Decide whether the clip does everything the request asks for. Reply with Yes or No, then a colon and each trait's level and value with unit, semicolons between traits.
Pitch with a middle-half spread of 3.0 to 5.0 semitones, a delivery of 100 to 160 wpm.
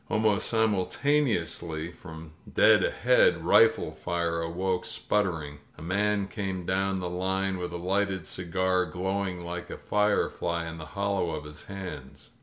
No: narrow, 2.6 semitones; average, 140 wpm